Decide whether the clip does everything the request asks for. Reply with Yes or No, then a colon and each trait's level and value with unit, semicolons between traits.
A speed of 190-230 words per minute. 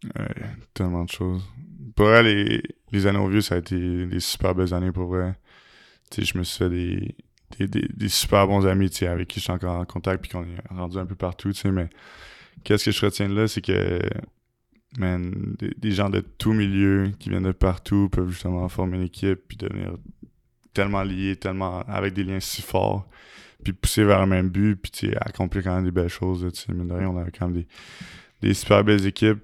Yes: average, 215 wpm